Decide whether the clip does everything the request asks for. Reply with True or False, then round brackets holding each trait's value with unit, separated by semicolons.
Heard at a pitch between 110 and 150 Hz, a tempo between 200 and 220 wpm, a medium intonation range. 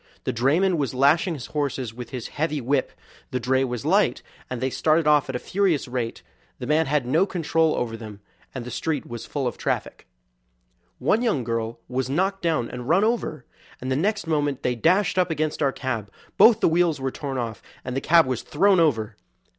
True (140 Hz; 205 wpm; 4.7 semitones)